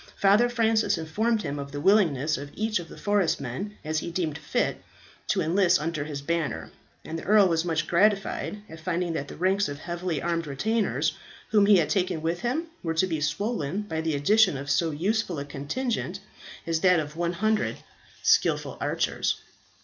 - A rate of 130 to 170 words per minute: No, average, 185 wpm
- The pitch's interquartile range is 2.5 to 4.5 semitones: No, average, 4.9 semitones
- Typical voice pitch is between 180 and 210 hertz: No, medium, 170 Hz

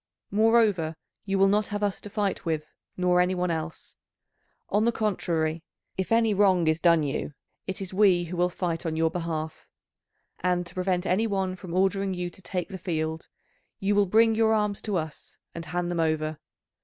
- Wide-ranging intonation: No, average, 3.3 semitones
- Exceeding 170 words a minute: Yes, average, 190 wpm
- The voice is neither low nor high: Yes, medium, 180 Hz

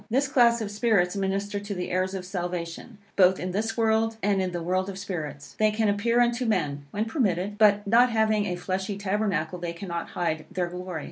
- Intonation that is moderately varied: Yes, average, 3.5 semitones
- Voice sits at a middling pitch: No, high, 195 Hz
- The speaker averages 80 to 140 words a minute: No, fast, 205 wpm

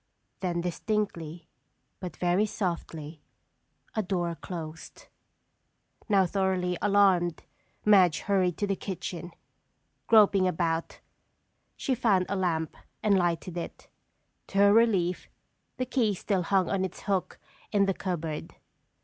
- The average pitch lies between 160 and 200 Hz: Yes, medium, 185 Hz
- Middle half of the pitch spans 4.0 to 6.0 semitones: No, average, 2.7 semitones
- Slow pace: Yes, slow, 120 wpm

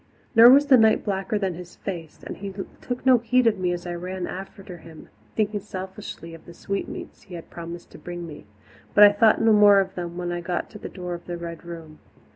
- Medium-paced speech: No, fast, 235 wpm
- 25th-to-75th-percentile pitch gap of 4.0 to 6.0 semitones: No, average, 3.3 semitones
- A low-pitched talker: No, medium, 185 Hz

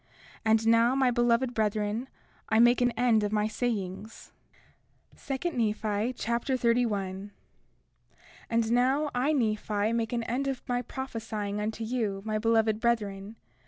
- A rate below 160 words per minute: Yes, average, 140 wpm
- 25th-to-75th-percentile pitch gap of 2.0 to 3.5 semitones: Yes, narrow, 2.5 semitones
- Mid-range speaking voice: No, high, 230 Hz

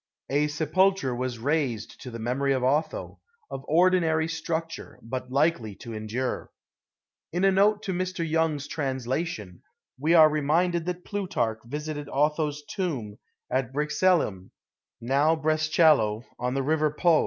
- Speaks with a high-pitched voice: No, medium, 150 Hz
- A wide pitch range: No, average, 4.3 semitones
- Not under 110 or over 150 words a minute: Yes, slow, 135 wpm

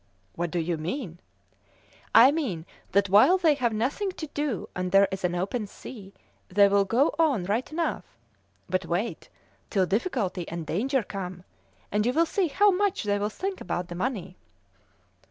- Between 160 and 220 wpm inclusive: Yes, average, 170 wpm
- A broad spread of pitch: Yes, wide, 7.3 semitones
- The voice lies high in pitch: Yes, high, 205 Hz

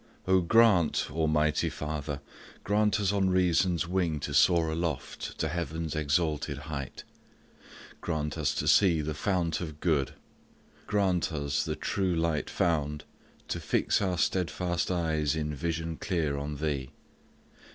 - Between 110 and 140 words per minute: Yes, slow, 135 wpm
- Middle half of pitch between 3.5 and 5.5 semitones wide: No, average, 3.1 semitones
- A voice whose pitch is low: Yes, very low, 80 Hz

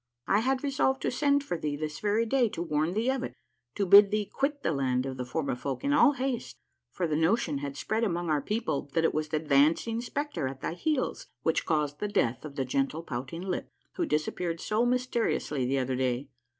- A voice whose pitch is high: No, medium, 170 Hz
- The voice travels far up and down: Yes, wide, 8.5 semitones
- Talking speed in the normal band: No, fast, 220 wpm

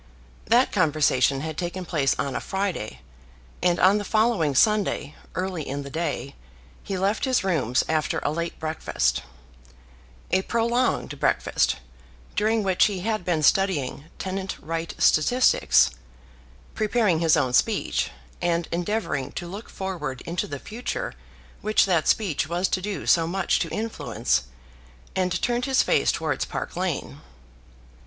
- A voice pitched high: No, medium, 180 Hz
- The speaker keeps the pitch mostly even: No, average, 5.0 semitones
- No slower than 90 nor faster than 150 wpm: Yes, average, 140 wpm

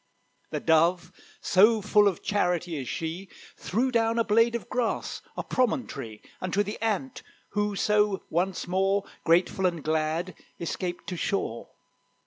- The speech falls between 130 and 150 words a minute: Yes, average, 140 wpm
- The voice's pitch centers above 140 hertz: Yes, high, 190 Hz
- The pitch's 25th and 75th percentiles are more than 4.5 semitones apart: No, average, 3.7 semitones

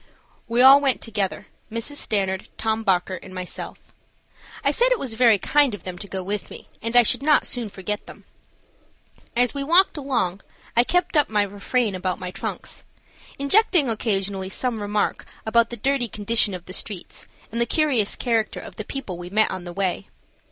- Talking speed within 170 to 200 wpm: Yes, average, 185 wpm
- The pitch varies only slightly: No, average, 4.8 semitones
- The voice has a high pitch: Yes, high, 220 Hz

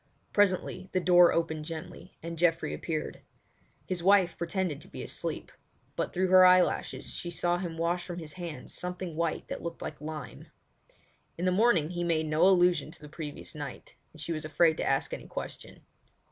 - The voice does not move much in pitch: Yes, narrow, 2.3 semitones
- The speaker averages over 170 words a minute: Yes, average, 185 wpm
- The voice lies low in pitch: No, medium, 170 Hz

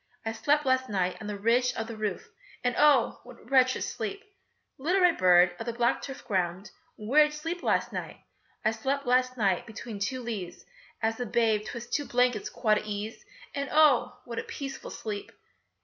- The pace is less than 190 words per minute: No, average, 195 wpm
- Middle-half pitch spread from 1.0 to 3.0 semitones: No, average, 4.2 semitones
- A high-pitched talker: Yes, high, 235 Hz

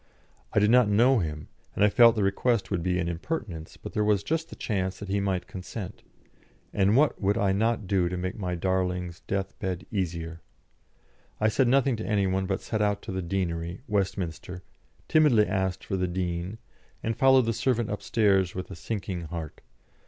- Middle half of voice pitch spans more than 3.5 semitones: No, average, 3.2 semitones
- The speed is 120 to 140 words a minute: No, average, 190 wpm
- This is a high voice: No, very low, 95 Hz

